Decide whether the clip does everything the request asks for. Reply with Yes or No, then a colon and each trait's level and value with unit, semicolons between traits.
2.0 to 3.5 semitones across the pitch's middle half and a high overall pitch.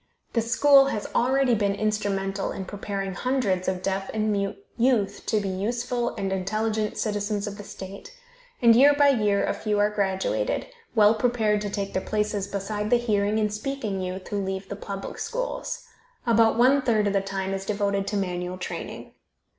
Yes: average, 2.7 semitones; high, 210 Hz